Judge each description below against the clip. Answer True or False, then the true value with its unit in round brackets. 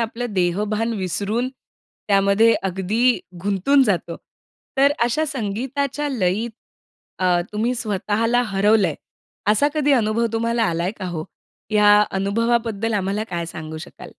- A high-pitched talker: True (215 Hz)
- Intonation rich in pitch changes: False (3.5 semitones)